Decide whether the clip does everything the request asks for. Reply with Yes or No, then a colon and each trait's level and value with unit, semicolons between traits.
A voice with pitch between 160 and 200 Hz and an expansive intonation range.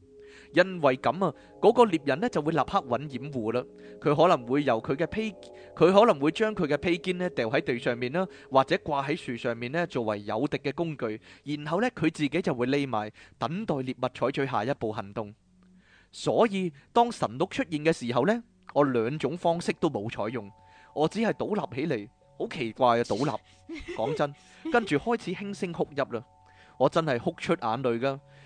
No: medium, 145 Hz; wide, 6.5 semitones